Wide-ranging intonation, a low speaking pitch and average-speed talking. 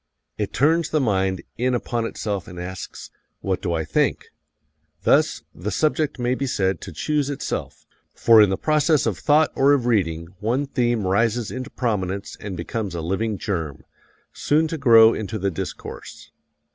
Yes: wide, 5.9 semitones; low, 110 Hz; average, 170 wpm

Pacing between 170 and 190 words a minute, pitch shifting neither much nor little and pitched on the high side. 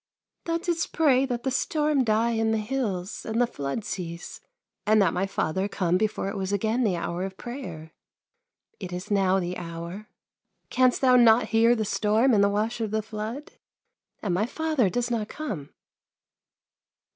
Yes: average, 180 wpm; average, 4.4 semitones; high, 215 Hz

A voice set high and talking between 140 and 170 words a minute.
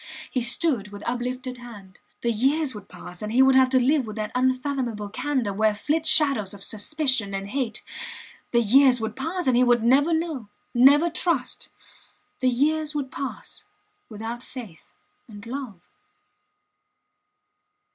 Yes: very high, 250 Hz; average, 150 wpm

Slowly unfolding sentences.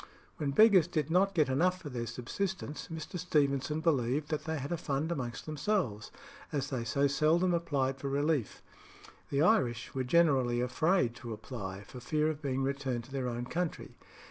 No: average, 175 wpm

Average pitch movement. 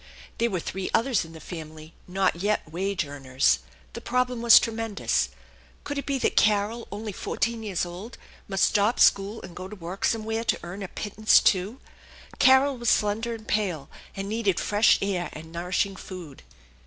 Yes: average, 4.1 semitones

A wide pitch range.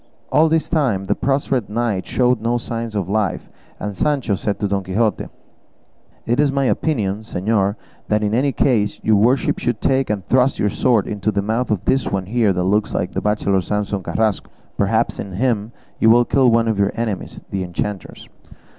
No: average, 3.4 semitones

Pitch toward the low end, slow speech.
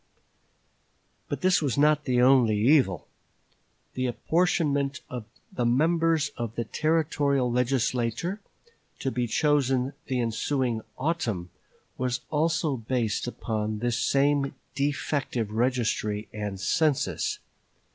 Yes: low, 130 Hz; slow, 105 wpm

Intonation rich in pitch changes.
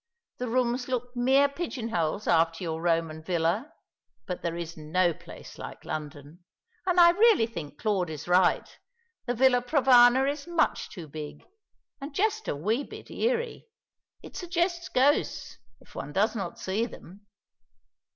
Yes: wide, 8.7 semitones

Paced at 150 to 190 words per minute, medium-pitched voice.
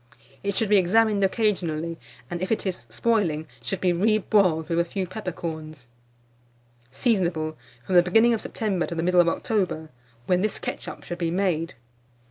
Yes: average, 165 wpm; medium, 180 Hz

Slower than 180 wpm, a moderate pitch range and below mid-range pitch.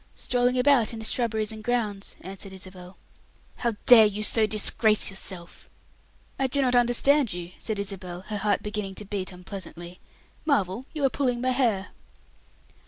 No: average, 160 wpm; average, 4.2 semitones; high, 215 Hz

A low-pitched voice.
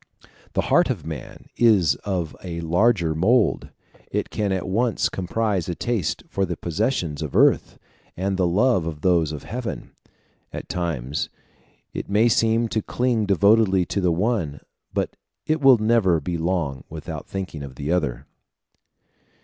Yes: very low, 95 Hz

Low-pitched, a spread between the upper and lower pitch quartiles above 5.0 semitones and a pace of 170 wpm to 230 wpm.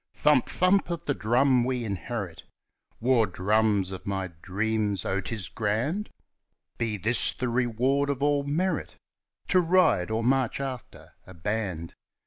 No: low, 115 Hz; wide, 5.4 semitones; average, 140 wpm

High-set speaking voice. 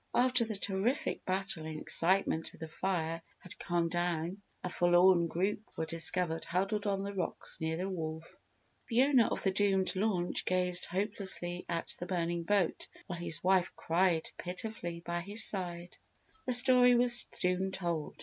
No: medium, 180 Hz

